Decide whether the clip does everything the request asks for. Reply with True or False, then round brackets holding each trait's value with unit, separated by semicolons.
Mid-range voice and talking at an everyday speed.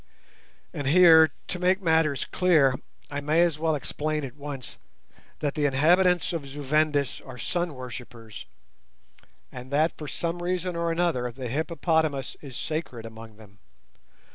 True (150 Hz; 145 wpm)